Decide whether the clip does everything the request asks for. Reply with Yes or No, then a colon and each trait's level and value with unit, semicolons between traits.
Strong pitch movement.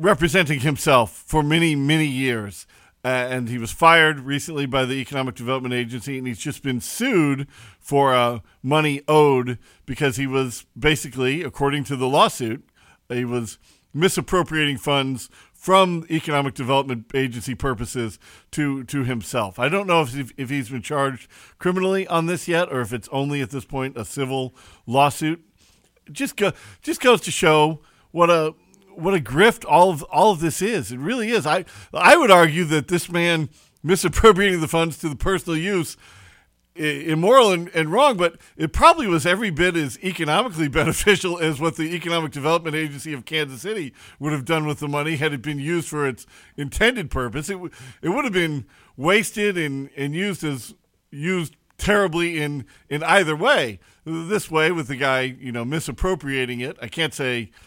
No: average, 4.6 semitones